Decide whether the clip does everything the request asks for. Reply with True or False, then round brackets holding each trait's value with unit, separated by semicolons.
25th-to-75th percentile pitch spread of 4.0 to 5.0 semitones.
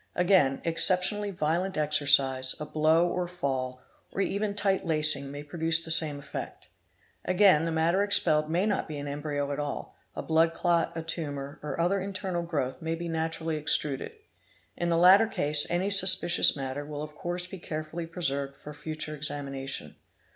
False (3.4 semitones)